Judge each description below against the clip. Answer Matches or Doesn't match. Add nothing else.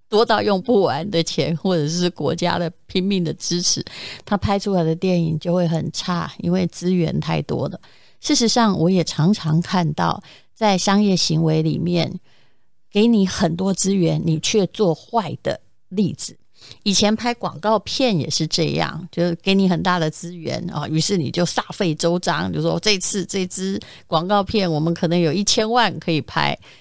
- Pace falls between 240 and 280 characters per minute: Matches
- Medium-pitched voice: Matches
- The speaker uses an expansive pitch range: Doesn't match